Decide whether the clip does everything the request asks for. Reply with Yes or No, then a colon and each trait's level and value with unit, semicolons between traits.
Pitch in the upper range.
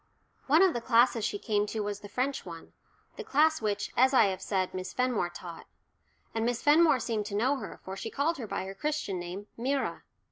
Yes: high, 225 Hz